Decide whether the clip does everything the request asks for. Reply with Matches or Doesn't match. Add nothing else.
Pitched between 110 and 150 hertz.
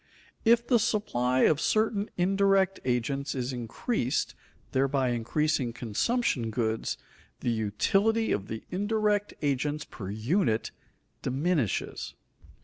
Matches